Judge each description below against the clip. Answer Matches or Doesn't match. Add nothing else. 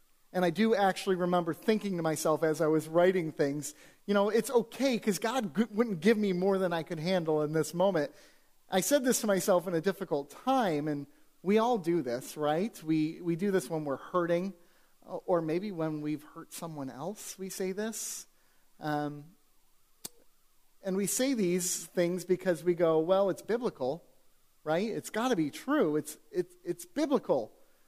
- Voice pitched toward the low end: Doesn't match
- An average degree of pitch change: Matches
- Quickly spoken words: Doesn't match